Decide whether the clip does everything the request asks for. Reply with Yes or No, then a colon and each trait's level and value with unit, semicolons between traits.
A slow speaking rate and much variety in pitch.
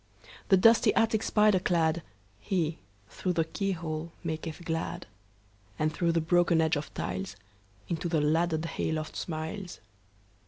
Yes: slow, 120 wpm; wide, 8.9 semitones